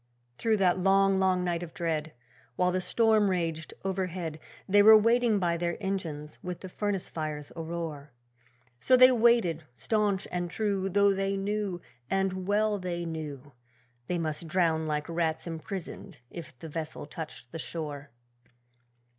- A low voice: No, medium, 180 Hz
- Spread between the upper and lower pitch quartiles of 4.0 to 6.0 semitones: No, average, 3.5 semitones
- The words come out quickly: No, average, 150 wpm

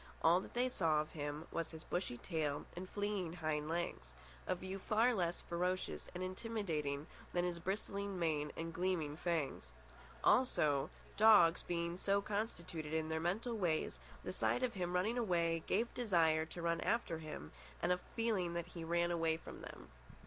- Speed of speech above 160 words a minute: Yes, average, 170 wpm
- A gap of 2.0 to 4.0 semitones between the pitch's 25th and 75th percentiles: Yes, average, 3.4 semitones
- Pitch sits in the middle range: Yes, medium, 170 Hz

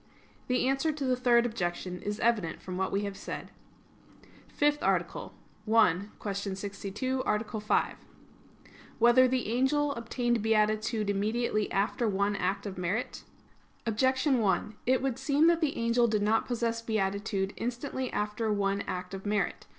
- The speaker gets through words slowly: No, average, 150 wpm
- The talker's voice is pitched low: No, high, 220 Hz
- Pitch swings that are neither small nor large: Yes, average, 3.8 semitones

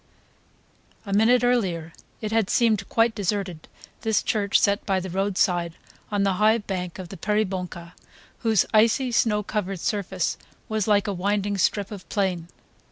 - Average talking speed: Yes, average, 155 wpm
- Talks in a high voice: Yes, high, 200 Hz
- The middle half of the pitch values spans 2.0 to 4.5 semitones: Yes, narrow, 2.6 semitones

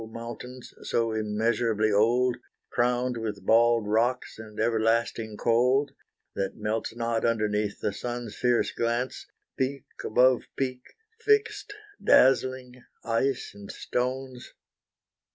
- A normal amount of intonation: No, narrow, 2.3 semitones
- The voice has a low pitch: Yes, low, 120 Hz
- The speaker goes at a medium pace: No, slow, 105 wpm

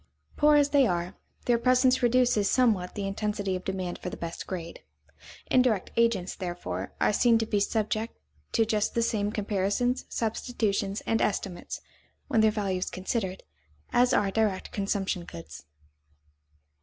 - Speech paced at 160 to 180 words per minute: No, average, 150 wpm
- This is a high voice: Yes, high, 210 Hz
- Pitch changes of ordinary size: Yes, average, 3.6 semitones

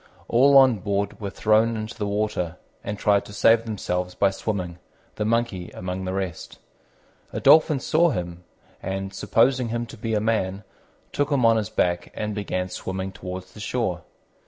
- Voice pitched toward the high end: No, low, 105 Hz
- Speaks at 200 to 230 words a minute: No, average, 175 wpm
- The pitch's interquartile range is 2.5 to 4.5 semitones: Yes, average, 3.5 semitones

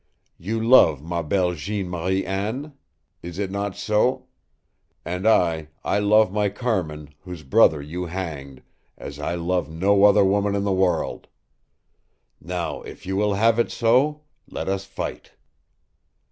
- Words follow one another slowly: No, average, 145 wpm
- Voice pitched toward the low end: Yes, very low, 95 Hz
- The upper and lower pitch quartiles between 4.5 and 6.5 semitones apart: No, average, 3.4 semitones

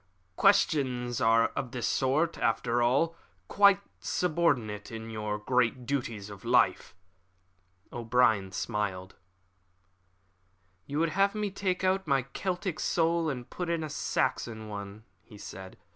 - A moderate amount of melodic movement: No, wide, 7.3 semitones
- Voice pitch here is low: Yes, low, 125 Hz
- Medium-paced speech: No, slow, 130 wpm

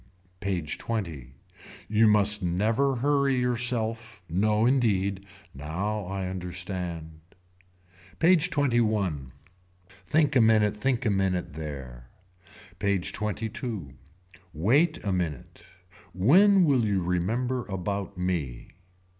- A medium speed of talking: No, slow, 100 wpm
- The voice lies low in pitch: Yes, low, 100 Hz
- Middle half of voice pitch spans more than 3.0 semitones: Yes, average, 5.0 semitones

